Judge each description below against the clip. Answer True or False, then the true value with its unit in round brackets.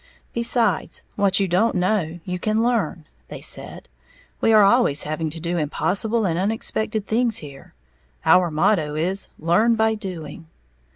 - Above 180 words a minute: False (150 wpm)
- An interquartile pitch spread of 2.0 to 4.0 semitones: False (5.1 semitones)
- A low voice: False (190 Hz)